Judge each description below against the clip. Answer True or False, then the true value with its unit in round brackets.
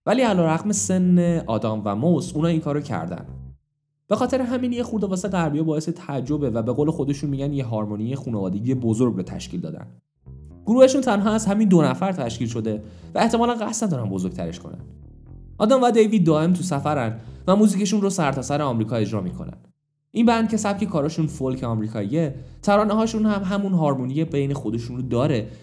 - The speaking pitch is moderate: True (150 Hz)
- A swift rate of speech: True (180 wpm)